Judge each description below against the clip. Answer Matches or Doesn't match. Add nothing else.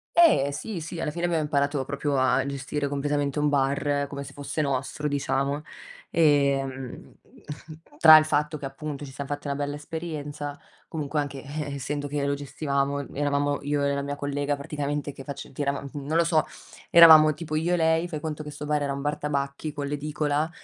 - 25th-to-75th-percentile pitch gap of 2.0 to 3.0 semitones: Doesn't match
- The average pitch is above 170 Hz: Doesn't match